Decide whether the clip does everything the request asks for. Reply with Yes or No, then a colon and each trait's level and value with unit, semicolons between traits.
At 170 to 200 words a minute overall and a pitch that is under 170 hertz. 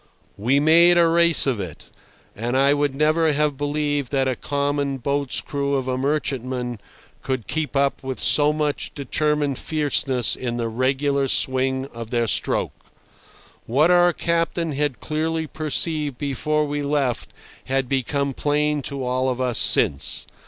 No: average, 150 wpm; medium, 140 Hz